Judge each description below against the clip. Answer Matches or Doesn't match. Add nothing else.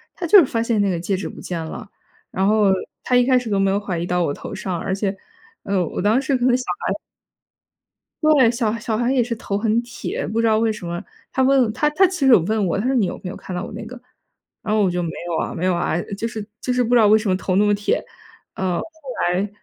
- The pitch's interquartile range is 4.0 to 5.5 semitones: Matches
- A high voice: Matches